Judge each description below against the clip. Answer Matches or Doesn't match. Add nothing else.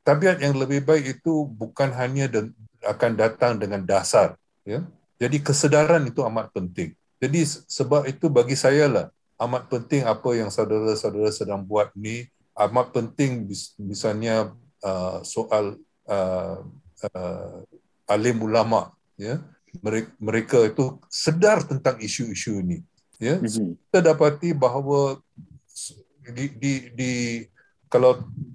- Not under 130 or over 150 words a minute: Doesn't match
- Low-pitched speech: Matches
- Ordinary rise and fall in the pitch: Matches